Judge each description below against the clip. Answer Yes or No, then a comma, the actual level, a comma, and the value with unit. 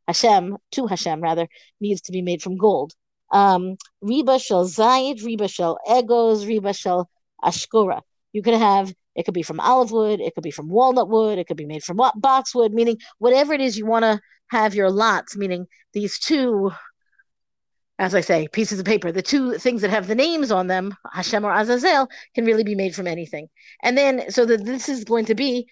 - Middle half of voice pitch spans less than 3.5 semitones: No, average, 4.6 semitones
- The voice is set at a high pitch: Yes, high, 215 Hz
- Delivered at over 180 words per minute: Yes, average, 200 wpm